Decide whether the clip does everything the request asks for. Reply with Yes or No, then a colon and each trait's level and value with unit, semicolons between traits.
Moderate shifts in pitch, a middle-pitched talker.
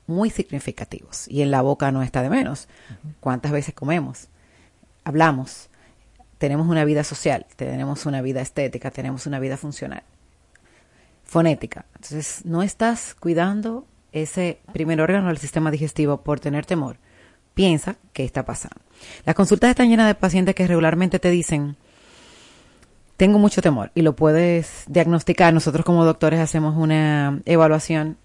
Yes: average, 3.7 semitones; medium, 155 Hz